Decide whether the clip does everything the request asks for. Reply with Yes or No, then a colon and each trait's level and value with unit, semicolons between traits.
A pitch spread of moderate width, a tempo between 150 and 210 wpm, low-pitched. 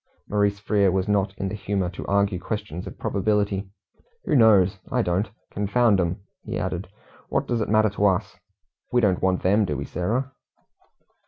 No: narrow, 2.1 semitones; average, 175 wpm; low, 100 Hz